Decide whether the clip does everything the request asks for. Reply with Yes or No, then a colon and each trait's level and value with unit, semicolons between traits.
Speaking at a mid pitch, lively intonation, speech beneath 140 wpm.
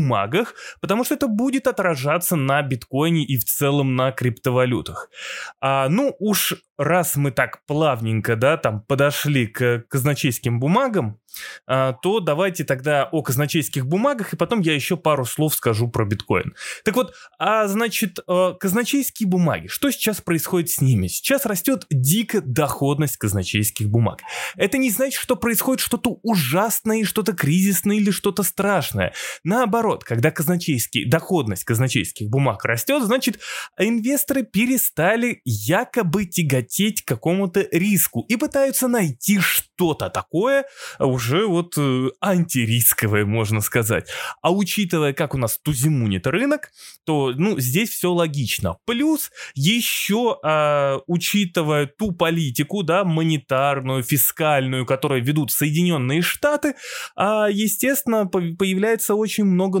Yes: medium, 170 Hz; wide, 7.7 semitones; average, 125 wpm